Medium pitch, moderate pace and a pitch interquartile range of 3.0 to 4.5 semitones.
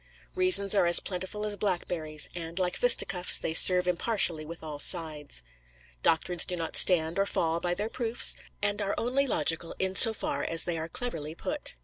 Yes: medium, 180 Hz; average, 185 wpm; average, 3.9 semitones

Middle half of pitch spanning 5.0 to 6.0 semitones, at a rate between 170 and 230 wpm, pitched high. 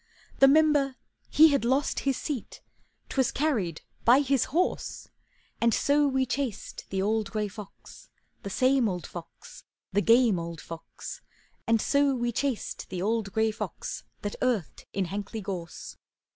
No: wide, 5.5 semitones; average, 150 wpm; high, 230 Hz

